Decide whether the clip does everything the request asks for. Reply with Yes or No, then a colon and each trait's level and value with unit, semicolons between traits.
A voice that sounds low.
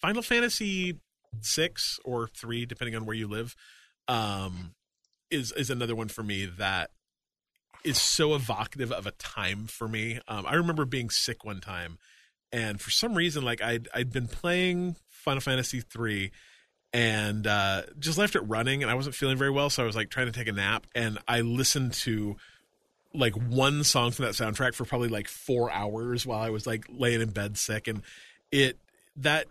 Yes: low, 120 Hz